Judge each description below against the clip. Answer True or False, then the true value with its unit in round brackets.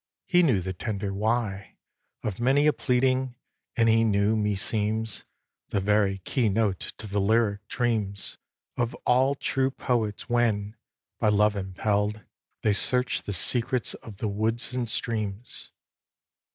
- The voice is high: False (110 Hz)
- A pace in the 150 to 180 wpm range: False (140 wpm)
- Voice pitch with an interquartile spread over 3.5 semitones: False (3.0 semitones)